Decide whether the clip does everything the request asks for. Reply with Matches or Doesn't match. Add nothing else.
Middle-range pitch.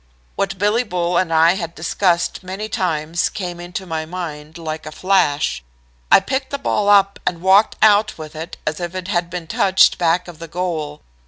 Matches